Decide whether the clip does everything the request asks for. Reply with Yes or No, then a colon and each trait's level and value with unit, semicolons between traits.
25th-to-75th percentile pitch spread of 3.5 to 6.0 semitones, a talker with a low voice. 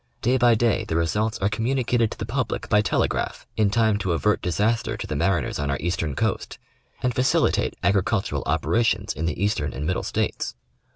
Yes: average, 5.0 semitones; low, 105 Hz